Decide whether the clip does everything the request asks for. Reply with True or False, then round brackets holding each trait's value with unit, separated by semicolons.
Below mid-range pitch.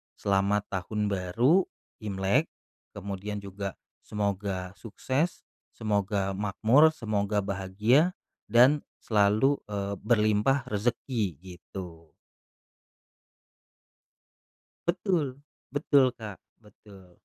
True (105 Hz)